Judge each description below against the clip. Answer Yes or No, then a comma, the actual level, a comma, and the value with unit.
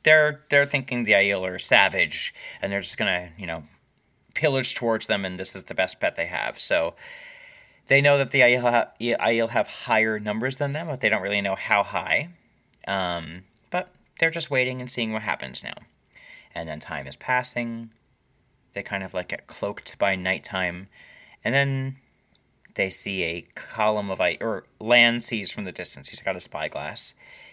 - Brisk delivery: No, average, 185 wpm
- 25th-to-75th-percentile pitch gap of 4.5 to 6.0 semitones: Yes, wide, 5.5 semitones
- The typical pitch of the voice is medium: No, low, 120 Hz